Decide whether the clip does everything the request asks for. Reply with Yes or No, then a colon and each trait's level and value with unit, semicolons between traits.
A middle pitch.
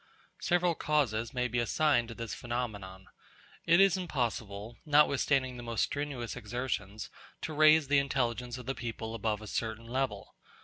No: low, 125 Hz